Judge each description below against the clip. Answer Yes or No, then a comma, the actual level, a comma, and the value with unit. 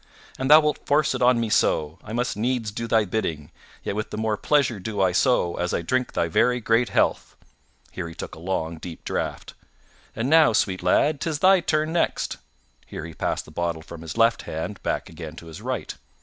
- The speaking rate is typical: No, fast, 215 wpm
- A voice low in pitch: Yes, low, 110 Hz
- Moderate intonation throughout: No, wide, 6.9 semitones